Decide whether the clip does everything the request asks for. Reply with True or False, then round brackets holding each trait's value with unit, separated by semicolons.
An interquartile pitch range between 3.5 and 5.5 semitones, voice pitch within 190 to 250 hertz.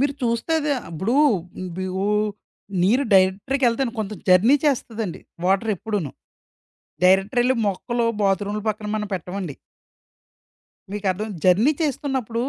True (4.2 semitones; 210 Hz)